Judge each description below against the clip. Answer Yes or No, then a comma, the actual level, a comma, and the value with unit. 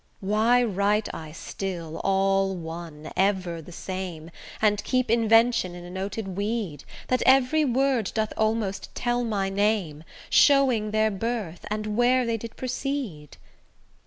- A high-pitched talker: Yes, high, 210 Hz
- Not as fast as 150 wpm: Yes, slow, 135 wpm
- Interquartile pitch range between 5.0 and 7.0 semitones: No, average, 3.9 semitones